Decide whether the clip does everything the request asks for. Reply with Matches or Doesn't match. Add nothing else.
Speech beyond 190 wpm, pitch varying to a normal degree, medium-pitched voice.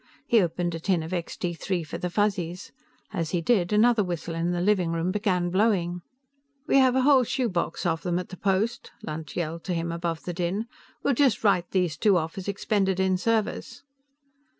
Matches